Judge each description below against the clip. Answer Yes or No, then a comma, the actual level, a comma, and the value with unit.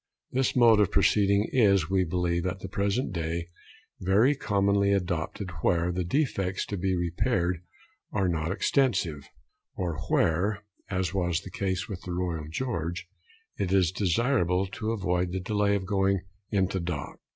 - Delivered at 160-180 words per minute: No, average, 150 wpm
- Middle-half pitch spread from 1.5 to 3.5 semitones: Yes, narrow, 2.5 semitones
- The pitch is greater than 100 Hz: No, very low, 95 Hz